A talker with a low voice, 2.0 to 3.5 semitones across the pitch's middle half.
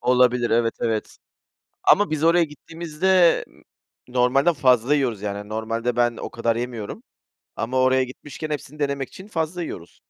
No: low, 130 Hz; average, 4.7 semitones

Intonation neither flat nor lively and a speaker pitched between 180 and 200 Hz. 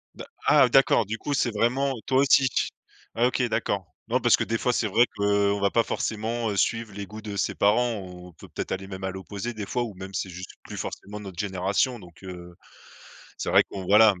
No: average, 3.6 semitones; low, 105 Hz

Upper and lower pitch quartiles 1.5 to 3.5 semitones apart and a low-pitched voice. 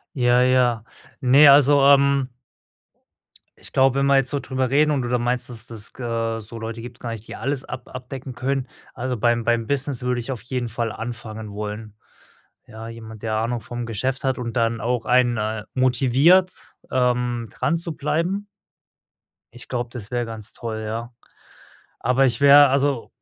Yes: average, 2.7 semitones; low, 125 Hz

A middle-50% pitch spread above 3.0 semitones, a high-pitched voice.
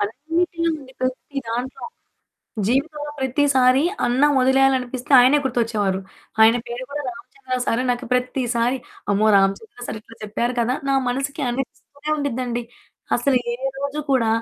No: average, 2.7 semitones; very high, 255 Hz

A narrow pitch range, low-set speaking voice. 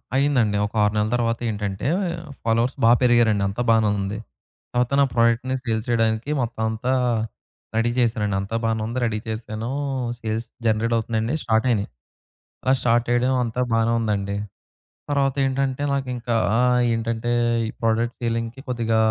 Yes: narrow, 1.7 semitones; low, 115 Hz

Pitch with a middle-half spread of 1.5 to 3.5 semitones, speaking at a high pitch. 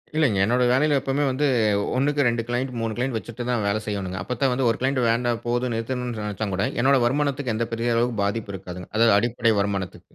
No: average, 3.1 semitones; low, 120 Hz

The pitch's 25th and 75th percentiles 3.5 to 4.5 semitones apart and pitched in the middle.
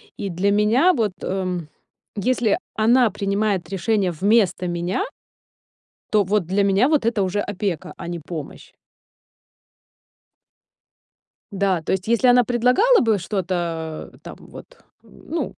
No: average, 3.9 semitones; high, 200 Hz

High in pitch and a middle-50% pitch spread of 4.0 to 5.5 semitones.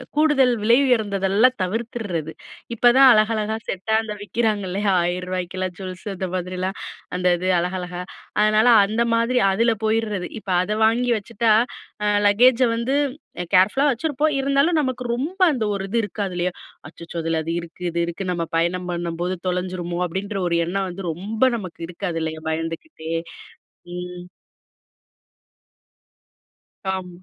Yes: high, 195 Hz; average, 4.5 semitones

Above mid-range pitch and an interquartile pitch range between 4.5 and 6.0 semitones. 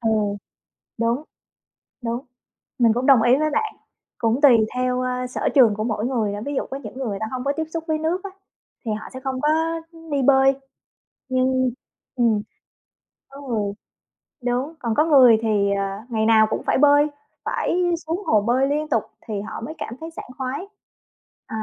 No: very high, 255 Hz; average, 3.9 semitones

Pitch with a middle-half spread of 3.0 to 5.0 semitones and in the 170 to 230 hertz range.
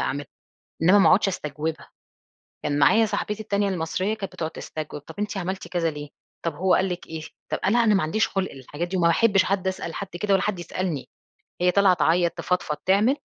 Yes: average, 3.7 semitones; medium, 185 Hz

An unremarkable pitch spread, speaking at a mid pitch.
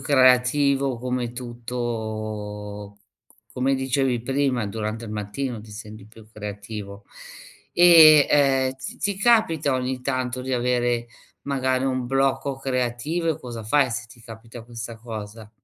No: average, 3.2 semitones; low, 125 Hz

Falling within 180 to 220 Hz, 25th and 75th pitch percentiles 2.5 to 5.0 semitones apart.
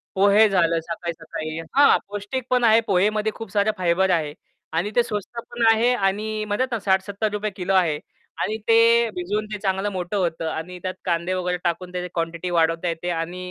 Yes: high, 190 Hz; average, 3.7 semitones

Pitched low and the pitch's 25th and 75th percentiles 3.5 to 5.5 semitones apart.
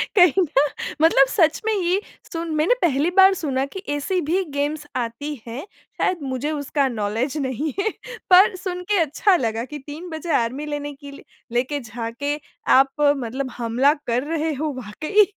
No: very high, 290 Hz; average, 4.2 semitones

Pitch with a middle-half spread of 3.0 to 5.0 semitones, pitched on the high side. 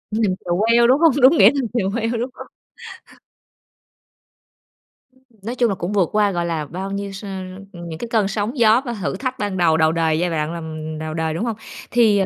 No: wide, 5.5 semitones; high, 200 Hz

